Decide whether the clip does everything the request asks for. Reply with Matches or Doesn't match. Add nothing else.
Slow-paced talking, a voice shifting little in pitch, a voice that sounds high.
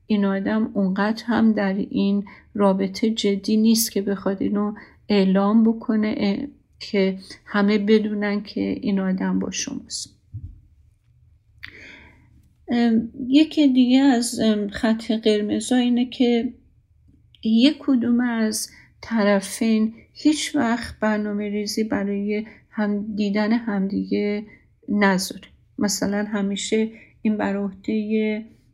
Matches